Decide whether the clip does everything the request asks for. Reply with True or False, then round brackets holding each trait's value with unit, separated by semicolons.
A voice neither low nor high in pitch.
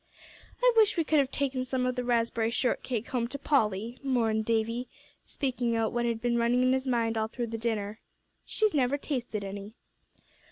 False (240 Hz)